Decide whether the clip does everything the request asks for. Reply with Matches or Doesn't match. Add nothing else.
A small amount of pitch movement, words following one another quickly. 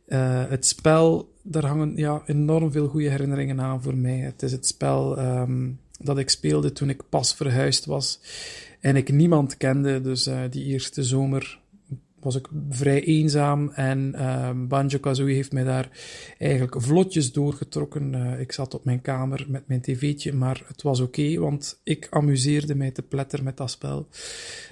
Doesn't match